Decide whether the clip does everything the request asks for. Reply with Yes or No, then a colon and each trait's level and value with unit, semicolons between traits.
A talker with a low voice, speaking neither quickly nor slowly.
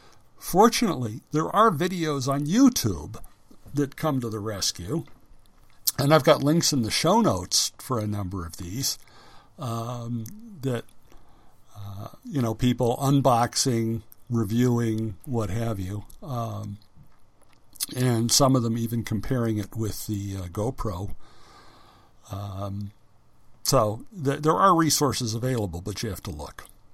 No: low, 115 Hz; slow, 130 wpm